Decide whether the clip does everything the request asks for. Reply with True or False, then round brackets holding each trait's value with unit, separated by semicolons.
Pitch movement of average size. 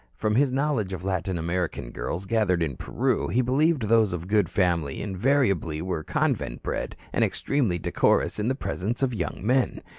False (6.1 semitones)